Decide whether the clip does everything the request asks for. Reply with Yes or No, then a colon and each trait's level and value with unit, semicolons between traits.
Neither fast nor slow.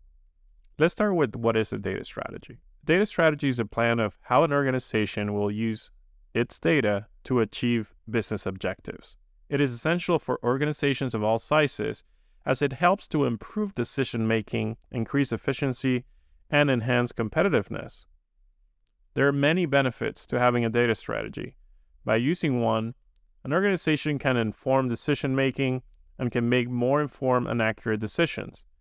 Yes: average, 150 wpm